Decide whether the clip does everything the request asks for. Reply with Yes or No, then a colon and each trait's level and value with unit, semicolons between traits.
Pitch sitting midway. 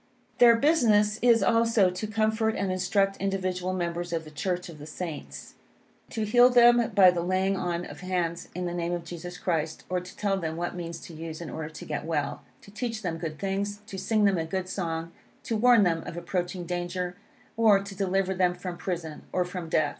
Yes: medium, 180 Hz